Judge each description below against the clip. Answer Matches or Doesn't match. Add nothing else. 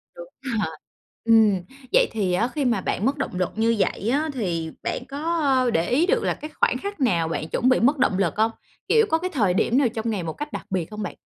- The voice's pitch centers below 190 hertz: Doesn't match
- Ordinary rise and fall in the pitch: Doesn't match